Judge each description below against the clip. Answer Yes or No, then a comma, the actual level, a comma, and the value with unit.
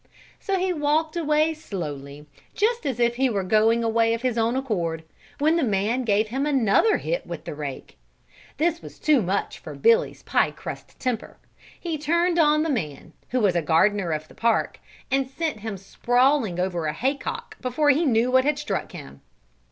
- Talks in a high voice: Yes, very high, 250 Hz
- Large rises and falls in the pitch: Yes, wide, 6.9 semitones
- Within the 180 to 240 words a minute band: Yes, average, 185 wpm